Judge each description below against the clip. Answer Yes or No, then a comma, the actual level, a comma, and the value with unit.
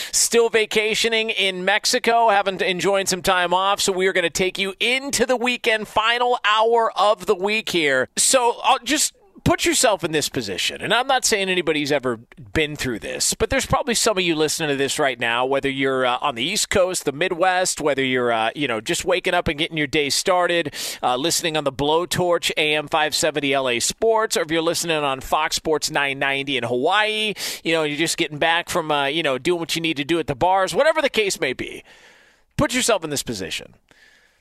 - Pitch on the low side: No, medium, 175 Hz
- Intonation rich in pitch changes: Yes, wide, 6.4 semitones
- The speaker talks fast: Yes, fast, 215 wpm